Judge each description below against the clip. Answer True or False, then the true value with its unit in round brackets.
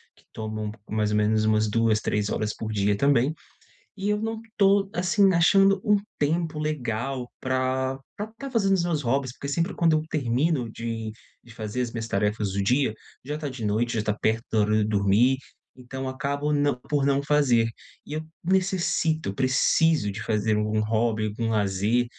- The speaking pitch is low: True (125 Hz)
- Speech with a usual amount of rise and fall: False (6.0 semitones)